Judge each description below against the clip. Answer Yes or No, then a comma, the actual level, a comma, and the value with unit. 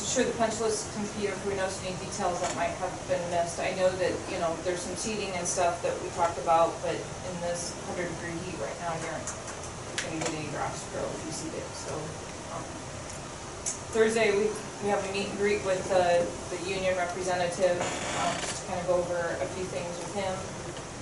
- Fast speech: Yes, fast, 210 wpm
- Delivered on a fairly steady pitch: Yes, narrow, 2.1 semitones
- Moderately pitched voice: Yes, medium, 180 Hz